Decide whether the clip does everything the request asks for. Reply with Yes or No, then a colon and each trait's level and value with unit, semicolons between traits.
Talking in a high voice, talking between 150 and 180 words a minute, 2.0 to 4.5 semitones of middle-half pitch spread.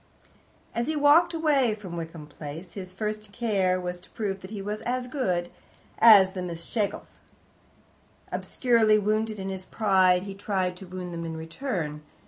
Yes: high, 195 Hz; average, 165 wpm; average, 3.6 semitones